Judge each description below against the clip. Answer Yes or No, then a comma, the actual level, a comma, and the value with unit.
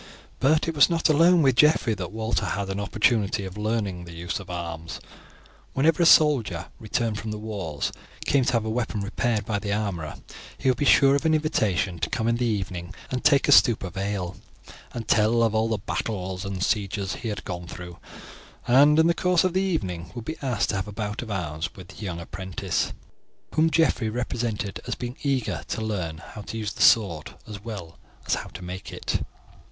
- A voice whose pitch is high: No, low, 110 Hz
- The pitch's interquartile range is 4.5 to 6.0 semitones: Yes, average, 4.9 semitones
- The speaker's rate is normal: No, fast, 210 wpm